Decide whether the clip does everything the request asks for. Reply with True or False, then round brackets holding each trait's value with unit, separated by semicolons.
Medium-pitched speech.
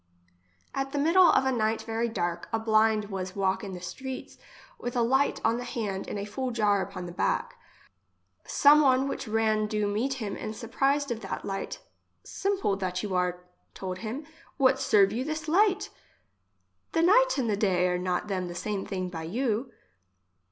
False (220 Hz)